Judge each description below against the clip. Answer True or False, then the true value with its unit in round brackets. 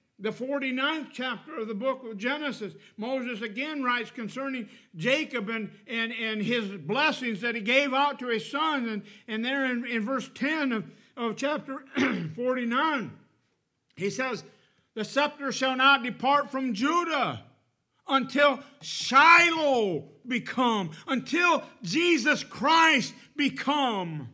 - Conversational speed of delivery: False (130 wpm)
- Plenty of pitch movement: False (3.7 semitones)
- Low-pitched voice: False (255 Hz)